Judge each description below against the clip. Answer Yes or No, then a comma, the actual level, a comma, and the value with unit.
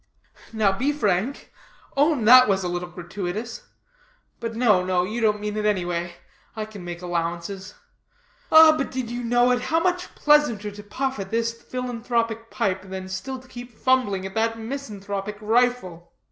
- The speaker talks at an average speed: Yes, average, 170 wpm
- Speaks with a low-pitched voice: No, high, 220 Hz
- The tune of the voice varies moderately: Yes, average, 4.6 semitones